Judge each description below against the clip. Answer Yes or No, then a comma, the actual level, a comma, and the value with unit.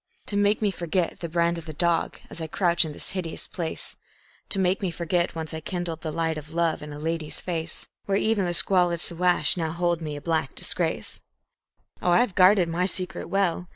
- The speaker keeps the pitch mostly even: Yes, narrow, 2.1 semitones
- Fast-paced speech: Yes, fast, 215 wpm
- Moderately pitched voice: Yes, medium, 170 Hz